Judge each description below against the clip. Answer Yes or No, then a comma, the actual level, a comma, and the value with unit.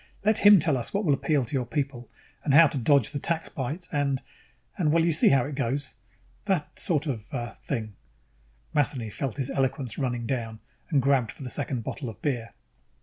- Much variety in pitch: No, average, 3.6 semitones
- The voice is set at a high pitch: No, medium, 140 Hz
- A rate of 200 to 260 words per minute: Yes, fast, 205 wpm